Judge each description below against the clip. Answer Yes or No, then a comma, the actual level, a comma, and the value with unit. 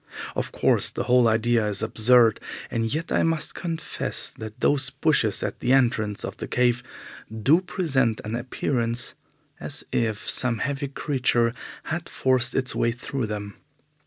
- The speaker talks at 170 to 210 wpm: No, average, 155 wpm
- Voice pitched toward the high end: No, low, 125 Hz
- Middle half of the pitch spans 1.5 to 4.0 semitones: Yes, average, 3.4 semitones